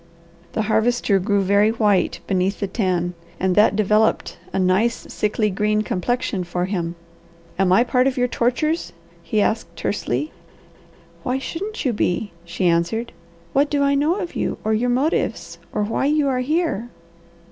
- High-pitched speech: Yes, high, 215 Hz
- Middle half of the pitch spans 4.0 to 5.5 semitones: Yes, average, 4.7 semitones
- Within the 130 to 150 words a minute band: No, average, 160 wpm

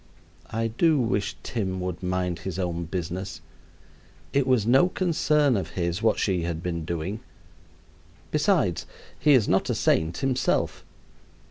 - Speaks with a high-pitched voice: No, very low, 95 Hz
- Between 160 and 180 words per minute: No, average, 140 wpm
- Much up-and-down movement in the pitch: Yes, wide, 6.6 semitones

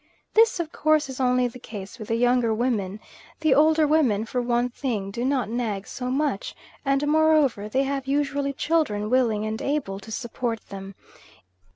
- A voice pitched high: Yes, very high, 250 Hz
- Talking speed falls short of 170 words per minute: No, average, 175 wpm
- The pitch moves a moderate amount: Yes, average, 4.4 semitones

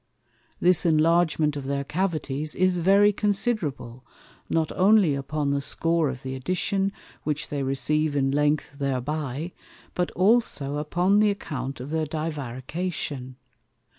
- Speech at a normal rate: No, slow, 130 wpm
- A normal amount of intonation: Yes, average, 4.5 semitones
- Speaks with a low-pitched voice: No, medium, 155 Hz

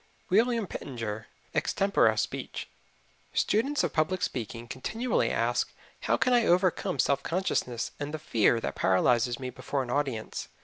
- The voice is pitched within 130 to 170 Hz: Yes, medium, 140 Hz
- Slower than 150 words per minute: Yes, average, 140 wpm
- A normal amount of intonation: No, wide, 8.2 semitones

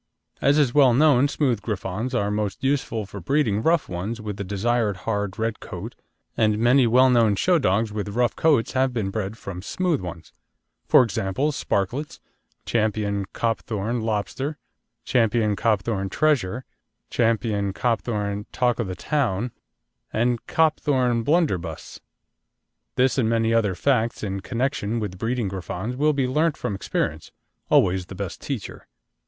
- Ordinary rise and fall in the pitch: Yes, average, 4.4 semitones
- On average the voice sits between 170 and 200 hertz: No, low, 115 Hz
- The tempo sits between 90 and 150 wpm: Yes, average, 145 wpm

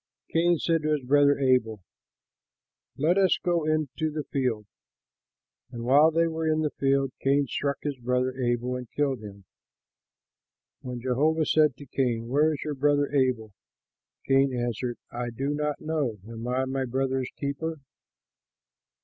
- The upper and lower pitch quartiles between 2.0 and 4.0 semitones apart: Yes, average, 3.3 semitones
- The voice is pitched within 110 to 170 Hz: Yes, low, 135 Hz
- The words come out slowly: No, average, 150 wpm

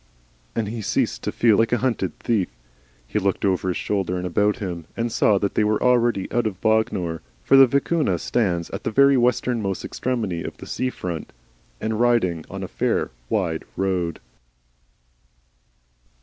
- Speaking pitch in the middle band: No, low, 105 Hz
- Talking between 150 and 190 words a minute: Yes, average, 170 wpm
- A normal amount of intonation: Yes, average, 4.6 semitones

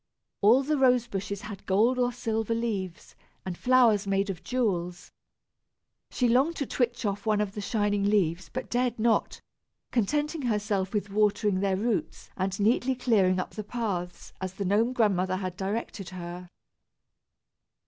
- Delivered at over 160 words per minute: No, average, 155 wpm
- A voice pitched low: No, high, 210 Hz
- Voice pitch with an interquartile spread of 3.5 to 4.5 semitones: Yes, average, 3.9 semitones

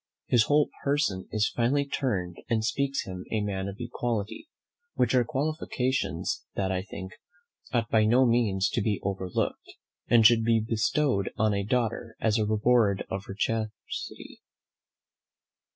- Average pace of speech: Yes, average, 150 wpm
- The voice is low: Yes, low, 110 Hz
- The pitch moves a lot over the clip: No, average, 3.7 semitones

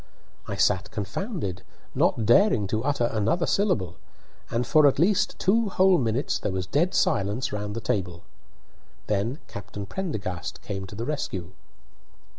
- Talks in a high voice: No, low, 110 Hz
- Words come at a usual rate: Yes, average, 145 wpm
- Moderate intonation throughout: No, wide, 7.9 semitones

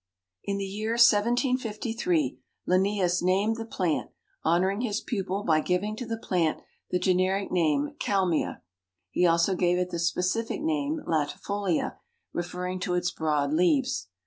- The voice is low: No, medium, 185 Hz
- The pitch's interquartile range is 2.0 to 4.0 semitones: Yes, average, 3.6 semitones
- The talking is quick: No, average, 140 wpm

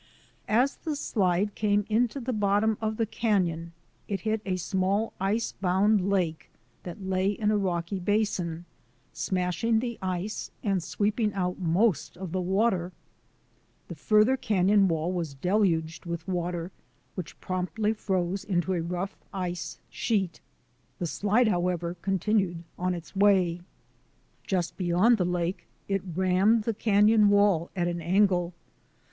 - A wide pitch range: No, average, 3.1 semitones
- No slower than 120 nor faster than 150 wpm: Yes, average, 140 wpm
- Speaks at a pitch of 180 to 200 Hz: Yes, high, 190 Hz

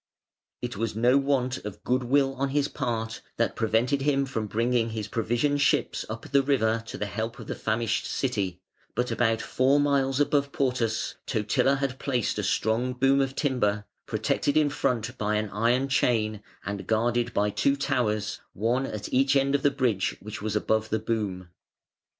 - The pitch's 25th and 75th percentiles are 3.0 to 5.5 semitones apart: Yes, average, 3.7 semitones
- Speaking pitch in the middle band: No, low, 120 Hz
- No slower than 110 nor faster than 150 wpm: No, average, 180 wpm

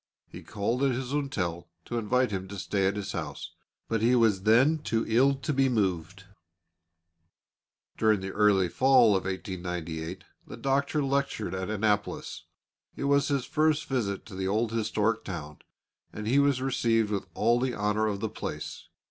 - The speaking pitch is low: Yes, low, 110 Hz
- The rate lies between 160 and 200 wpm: Yes, average, 170 wpm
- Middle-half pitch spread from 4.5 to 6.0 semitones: Yes, average, 5.1 semitones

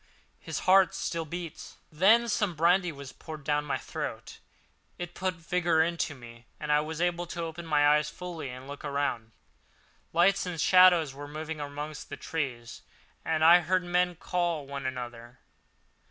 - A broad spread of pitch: No, average, 3.5 semitones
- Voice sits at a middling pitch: Yes, medium, 160 Hz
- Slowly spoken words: No, average, 170 wpm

